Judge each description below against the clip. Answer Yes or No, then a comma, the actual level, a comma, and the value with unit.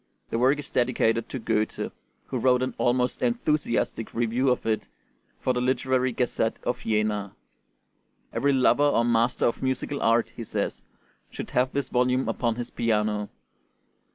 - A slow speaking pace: No, average, 155 wpm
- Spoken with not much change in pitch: Yes, narrow, 2.3 semitones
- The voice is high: No, low, 125 Hz